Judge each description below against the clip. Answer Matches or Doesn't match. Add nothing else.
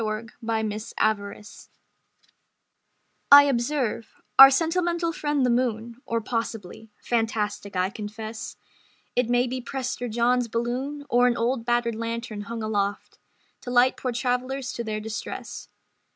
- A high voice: Matches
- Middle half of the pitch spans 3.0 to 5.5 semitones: Doesn't match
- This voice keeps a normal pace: Doesn't match